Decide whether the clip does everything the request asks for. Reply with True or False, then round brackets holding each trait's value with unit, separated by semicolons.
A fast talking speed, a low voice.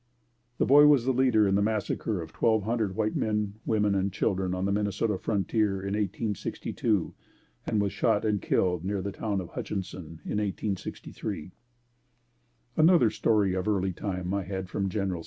False (170 wpm; 100 Hz)